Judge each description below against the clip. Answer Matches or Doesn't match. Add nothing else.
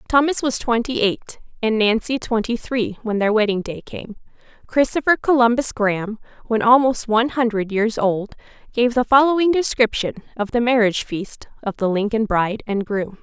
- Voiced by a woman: Matches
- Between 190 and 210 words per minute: Doesn't match